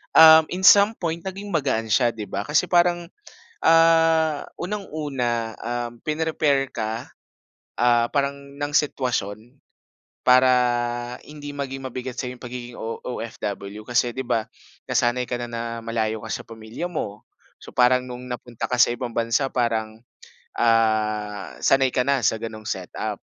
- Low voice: Yes, low, 125 Hz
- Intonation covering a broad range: No, average, 4.3 semitones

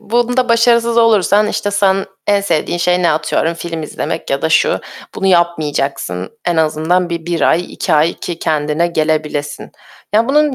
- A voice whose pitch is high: No, medium, 175 Hz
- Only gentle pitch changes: No, average, 4.9 semitones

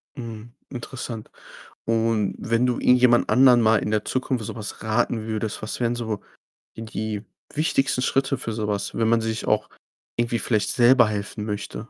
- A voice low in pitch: Yes, low, 115 Hz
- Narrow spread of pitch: Yes, narrow, 2.1 semitones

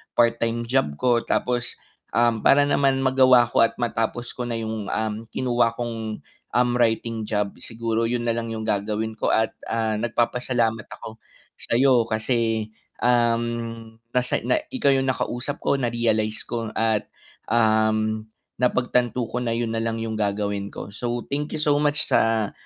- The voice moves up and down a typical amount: No, narrow, 1.8 semitones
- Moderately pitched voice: No, low, 115 Hz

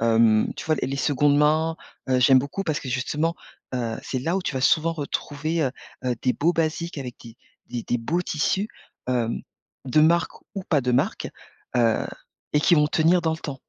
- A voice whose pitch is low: No, medium, 145 Hz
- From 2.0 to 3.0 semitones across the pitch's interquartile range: No, average, 4.3 semitones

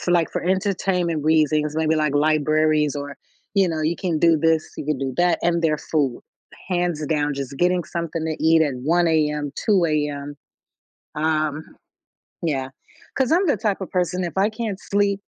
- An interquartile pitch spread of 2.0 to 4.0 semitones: Yes, average, 2.9 semitones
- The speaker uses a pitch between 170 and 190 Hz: No, medium, 160 Hz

